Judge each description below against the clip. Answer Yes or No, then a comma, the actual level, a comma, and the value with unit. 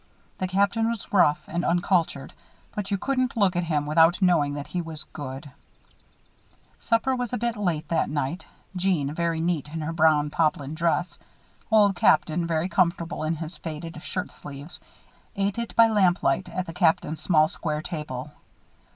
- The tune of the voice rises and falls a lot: No, average, 3.7 semitones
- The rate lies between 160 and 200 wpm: Yes, average, 165 wpm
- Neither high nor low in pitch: Yes, medium, 170 Hz